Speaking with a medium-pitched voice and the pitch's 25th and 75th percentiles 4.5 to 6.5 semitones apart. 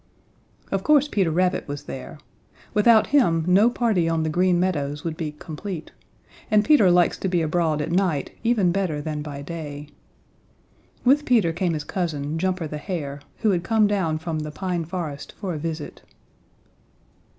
No: medium, 170 Hz; average, 4.1 semitones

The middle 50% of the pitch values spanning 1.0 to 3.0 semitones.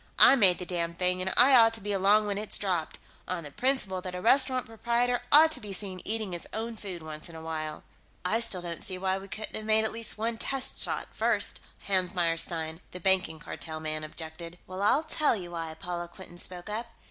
No: average, 4.4 semitones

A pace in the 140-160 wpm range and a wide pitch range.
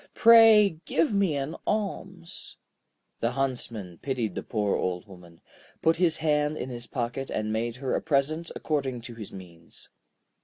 Yes: average, 155 wpm; wide, 6.4 semitones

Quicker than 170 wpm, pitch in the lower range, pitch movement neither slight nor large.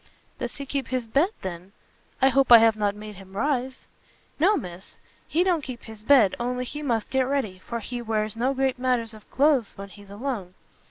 No: fast, 205 wpm; high, 240 Hz; average, 4.2 semitones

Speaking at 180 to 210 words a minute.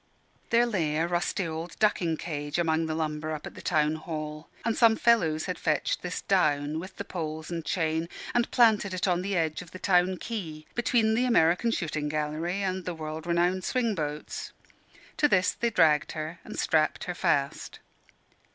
Yes: average, 185 wpm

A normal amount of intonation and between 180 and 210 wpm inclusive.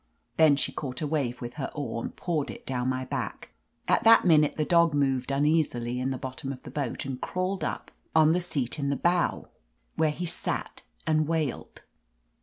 Yes: average, 3.6 semitones; average, 200 wpm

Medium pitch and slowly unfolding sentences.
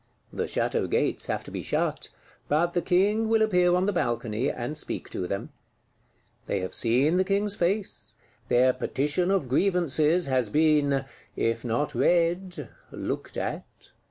No: medium, 160 Hz; average, 155 wpm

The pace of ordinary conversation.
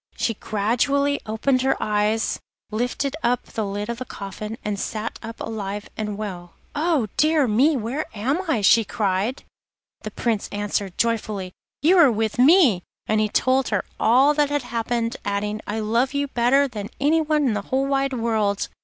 Yes: average, 170 wpm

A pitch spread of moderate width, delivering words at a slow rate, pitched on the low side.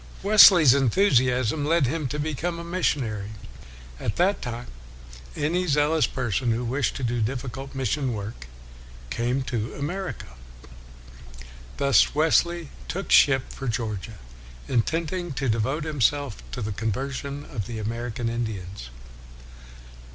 Yes: average, 4.7 semitones; slow, 125 wpm; low, 130 Hz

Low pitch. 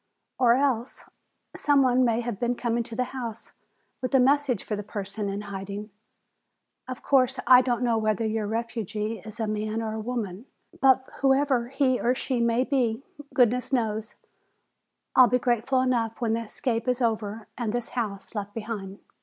No: high, 235 Hz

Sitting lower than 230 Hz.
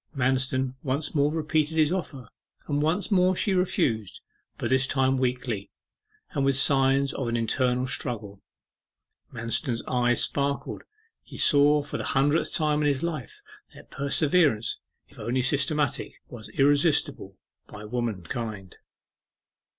Yes: low, 135 Hz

